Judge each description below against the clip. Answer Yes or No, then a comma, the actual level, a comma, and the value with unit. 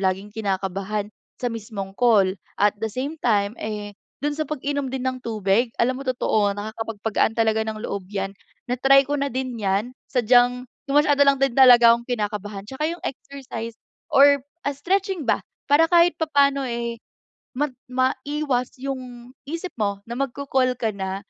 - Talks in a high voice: Yes, high, 245 Hz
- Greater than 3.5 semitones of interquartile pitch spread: Yes, average, 4.5 semitones